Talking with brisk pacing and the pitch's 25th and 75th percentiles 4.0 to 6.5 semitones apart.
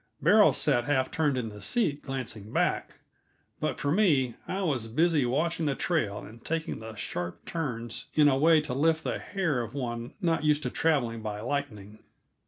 No: average, 185 wpm; wide, 5.6 semitones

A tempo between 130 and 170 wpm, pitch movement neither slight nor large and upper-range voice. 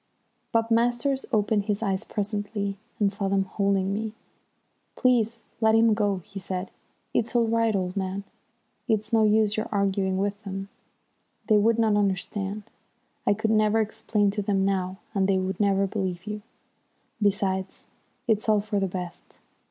No: average, 160 wpm; narrow, 2.1 semitones; high, 205 Hz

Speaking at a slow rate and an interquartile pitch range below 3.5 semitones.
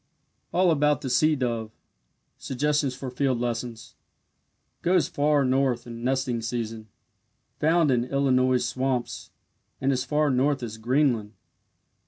Yes: slow, 125 wpm; average, 3.0 semitones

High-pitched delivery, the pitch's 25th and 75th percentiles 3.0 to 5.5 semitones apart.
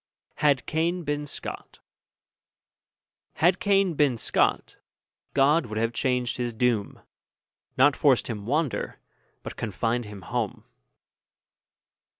No: low, 130 Hz; average, 4.4 semitones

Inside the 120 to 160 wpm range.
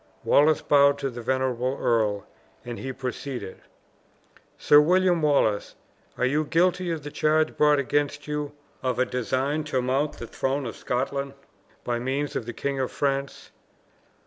Yes: average, 155 wpm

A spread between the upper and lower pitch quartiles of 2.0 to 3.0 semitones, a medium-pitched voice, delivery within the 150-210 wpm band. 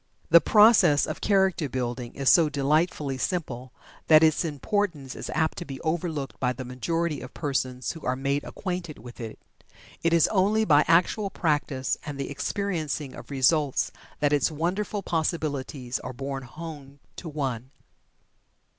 No: average, 4.0 semitones; medium, 150 Hz; average, 155 wpm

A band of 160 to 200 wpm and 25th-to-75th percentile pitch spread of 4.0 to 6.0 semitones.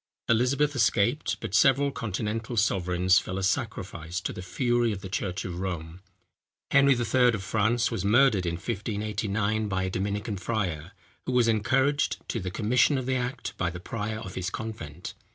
Yes: average, 170 wpm; average, 4.5 semitones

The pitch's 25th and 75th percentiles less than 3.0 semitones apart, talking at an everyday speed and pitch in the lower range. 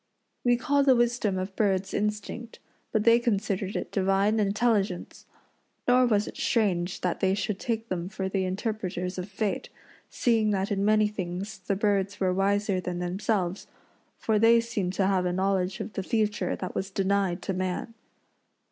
No: narrow, 2.4 semitones; average, 170 wpm; high, 200 Hz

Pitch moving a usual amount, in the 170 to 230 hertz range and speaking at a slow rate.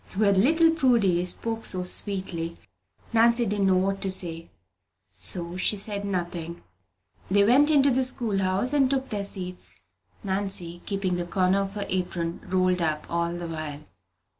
No: average, 3.8 semitones; high, 190 Hz; average, 160 wpm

